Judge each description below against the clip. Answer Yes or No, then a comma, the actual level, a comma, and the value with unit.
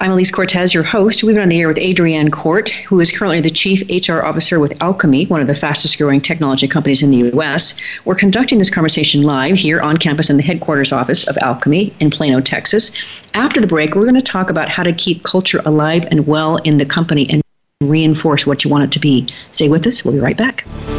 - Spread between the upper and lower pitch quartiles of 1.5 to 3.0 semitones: No, average, 3.7 semitones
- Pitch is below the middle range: No, medium, 160 Hz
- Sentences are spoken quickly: Yes, fast, 235 wpm